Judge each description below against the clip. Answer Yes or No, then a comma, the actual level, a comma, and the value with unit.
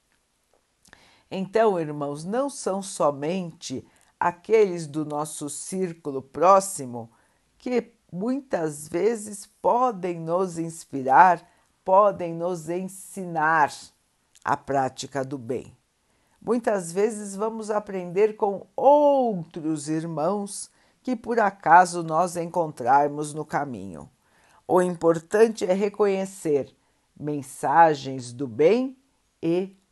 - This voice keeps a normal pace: No, slow, 90 wpm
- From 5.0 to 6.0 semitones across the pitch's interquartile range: Yes, wide, 5.4 semitones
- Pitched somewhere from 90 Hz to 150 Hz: No, medium, 175 Hz